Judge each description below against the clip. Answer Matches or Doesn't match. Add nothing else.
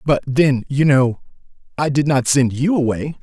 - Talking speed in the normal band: Matches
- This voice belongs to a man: Matches